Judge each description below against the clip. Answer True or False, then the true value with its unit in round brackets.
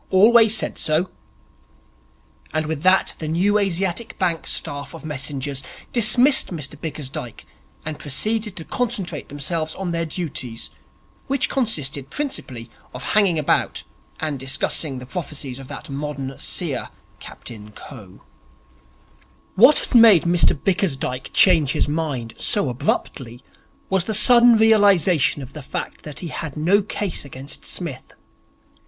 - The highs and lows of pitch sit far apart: True (6.2 semitones)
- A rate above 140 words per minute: False (135 wpm)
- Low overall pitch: False (160 Hz)